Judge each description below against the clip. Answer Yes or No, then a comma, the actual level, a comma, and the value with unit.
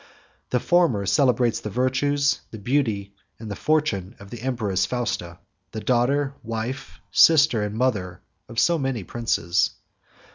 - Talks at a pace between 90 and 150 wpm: Yes, average, 140 wpm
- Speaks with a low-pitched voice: Yes, low, 120 Hz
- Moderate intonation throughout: Yes, average, 4.8 semitones